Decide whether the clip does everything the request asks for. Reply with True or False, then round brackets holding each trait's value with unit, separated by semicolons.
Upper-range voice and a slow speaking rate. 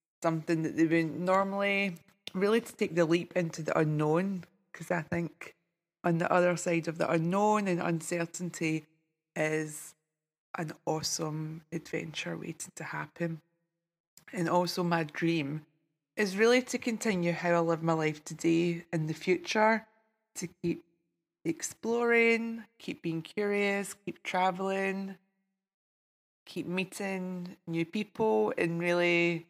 False (170 Hz; 130 wpm)